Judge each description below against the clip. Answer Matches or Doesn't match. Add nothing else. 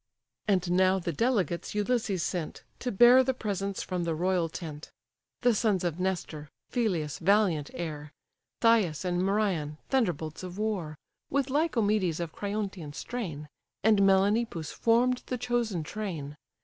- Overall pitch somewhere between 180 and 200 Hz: Matches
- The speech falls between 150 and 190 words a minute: Doesn't match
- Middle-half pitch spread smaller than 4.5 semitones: Doesn't match